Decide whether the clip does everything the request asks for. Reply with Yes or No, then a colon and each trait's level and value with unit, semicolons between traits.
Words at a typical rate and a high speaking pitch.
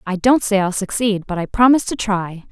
No: fast, 240 wpm; high, 205 Hz